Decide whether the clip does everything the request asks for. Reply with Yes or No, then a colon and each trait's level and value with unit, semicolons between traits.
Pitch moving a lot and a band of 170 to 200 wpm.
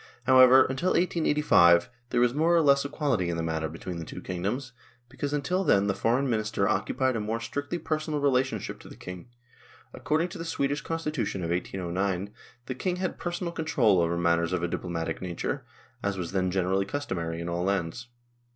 Yes: wide, 8.2 semitones; average, 185 wpm